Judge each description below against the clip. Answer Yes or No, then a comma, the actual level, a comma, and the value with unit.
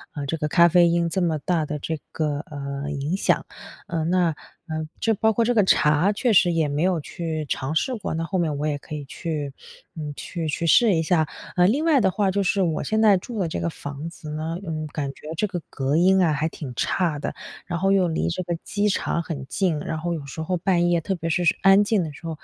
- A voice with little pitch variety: No, average, 3.5 semitones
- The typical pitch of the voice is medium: Yes, medium, 165 Hz